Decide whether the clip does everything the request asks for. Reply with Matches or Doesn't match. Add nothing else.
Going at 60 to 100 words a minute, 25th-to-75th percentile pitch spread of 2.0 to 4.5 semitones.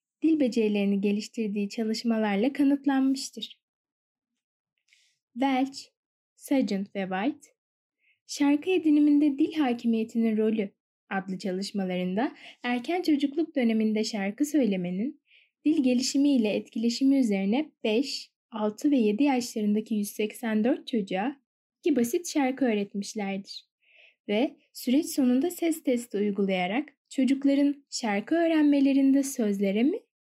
Doesn't match